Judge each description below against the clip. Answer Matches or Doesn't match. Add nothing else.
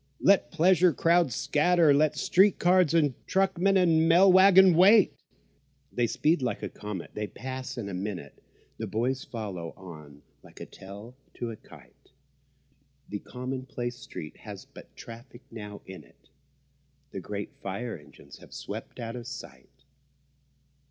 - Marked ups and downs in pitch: Matches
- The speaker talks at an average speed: Matches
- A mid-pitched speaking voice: Doesn't match